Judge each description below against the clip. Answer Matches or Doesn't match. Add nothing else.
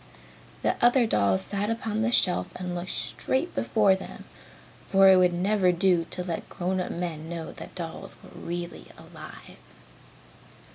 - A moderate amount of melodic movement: Matches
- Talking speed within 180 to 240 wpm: Doesn't match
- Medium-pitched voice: Matches